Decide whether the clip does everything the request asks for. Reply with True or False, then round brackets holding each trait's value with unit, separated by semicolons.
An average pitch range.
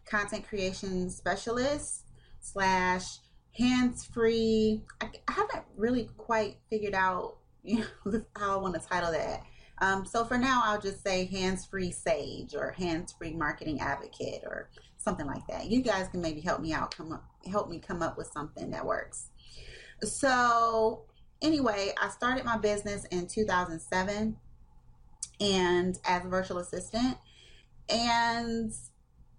True (3.8 semitones)